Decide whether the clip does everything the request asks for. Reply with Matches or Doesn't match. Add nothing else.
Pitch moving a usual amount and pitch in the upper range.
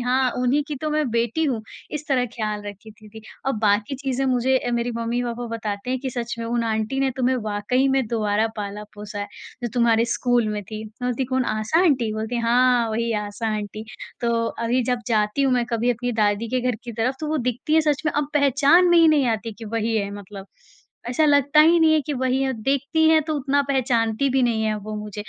Matches